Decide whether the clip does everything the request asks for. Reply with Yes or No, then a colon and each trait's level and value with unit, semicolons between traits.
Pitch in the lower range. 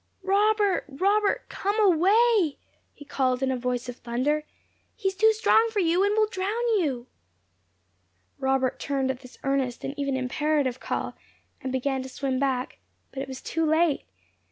No: very high, 290 Hz